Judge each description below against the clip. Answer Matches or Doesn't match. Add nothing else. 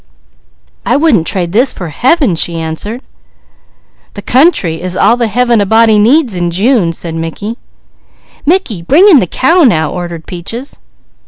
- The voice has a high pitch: Matches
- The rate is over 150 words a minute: Doesn't match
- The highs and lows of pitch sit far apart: Matches